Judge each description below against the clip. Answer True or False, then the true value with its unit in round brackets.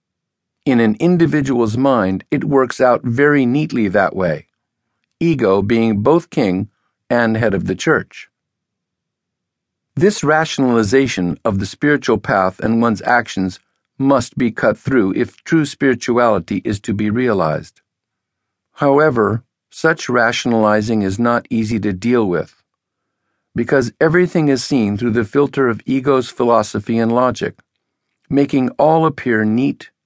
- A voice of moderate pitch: False (120 Hz)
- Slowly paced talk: True (130 wpm)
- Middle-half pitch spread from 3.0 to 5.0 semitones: True (3.8 semitones)